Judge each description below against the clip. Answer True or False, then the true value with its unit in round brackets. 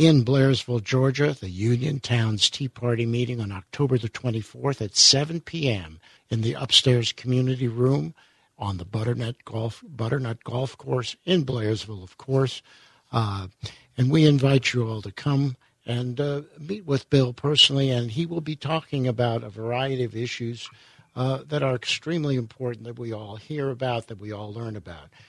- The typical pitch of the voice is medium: False (125 Hz)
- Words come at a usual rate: True (170 wpm)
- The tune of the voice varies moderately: True (3.2 semitones)